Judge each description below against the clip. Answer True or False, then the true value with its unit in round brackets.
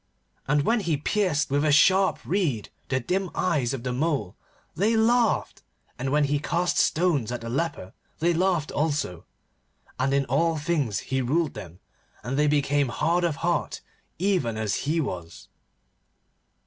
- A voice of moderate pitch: True (150 Hz)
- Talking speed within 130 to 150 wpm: False (160 wpm)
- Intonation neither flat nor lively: True (4.8 semitones)